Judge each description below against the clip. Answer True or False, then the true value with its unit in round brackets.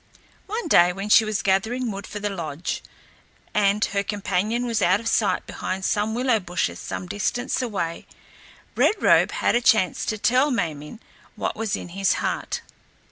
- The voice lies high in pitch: True (205 Hz)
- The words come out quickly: False (175 wpm)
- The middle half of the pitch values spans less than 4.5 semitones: True (3.7 semitones)